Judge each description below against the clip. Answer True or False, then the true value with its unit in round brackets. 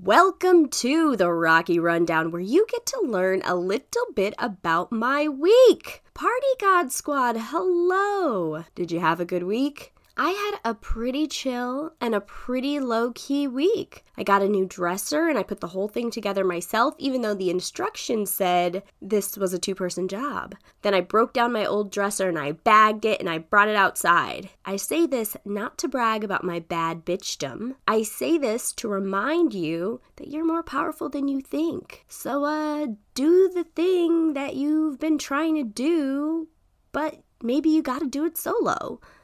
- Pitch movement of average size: False (8.1 semitones)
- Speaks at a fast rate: False (175 wpm)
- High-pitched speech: True (245 Hz)